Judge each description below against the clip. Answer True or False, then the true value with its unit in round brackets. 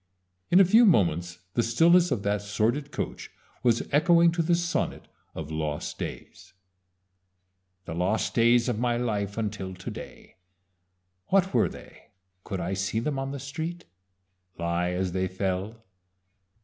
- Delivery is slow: False (150 wpm)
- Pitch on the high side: False (115 Hz)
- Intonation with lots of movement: True (8.1 semitones)